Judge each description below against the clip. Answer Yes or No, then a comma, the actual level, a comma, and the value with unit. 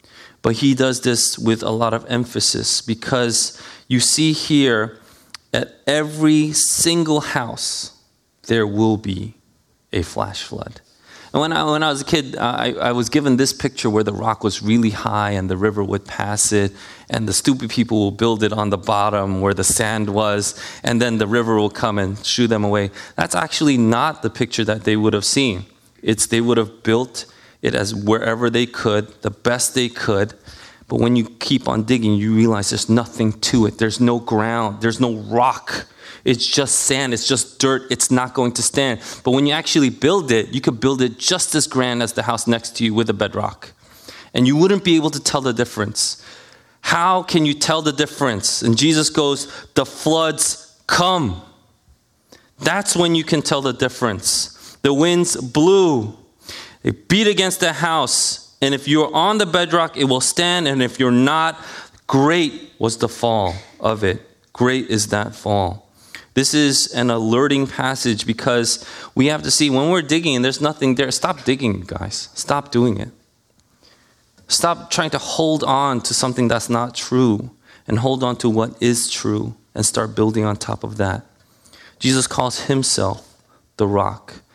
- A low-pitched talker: Yes, low, 120 Hz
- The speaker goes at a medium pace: Yes, average, 185 wpm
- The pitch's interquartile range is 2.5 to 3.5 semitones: No, average, 4.3 semitones